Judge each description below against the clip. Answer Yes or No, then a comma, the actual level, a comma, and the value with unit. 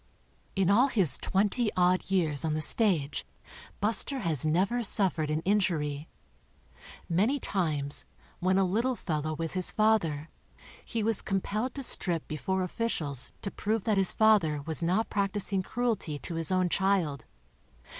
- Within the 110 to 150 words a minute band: Yes, average, 145 wpm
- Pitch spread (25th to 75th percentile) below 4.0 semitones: No, average, 5.1 semitones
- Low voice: No, medium, 185 Hz